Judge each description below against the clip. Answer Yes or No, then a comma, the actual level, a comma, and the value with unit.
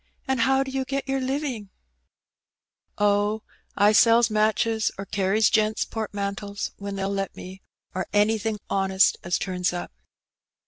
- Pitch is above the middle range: Yes, high, 210 Hz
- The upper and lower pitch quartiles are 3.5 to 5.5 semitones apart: No, narrow, 2.6 semitones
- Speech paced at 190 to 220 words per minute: No, average, 150 wpm